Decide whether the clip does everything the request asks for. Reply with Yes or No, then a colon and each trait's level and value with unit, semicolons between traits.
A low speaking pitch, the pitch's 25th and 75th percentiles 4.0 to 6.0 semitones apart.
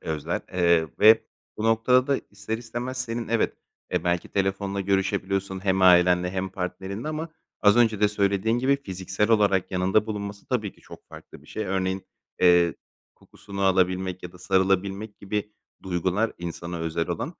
No: very low, 95 Hz; average, 2.7 semitones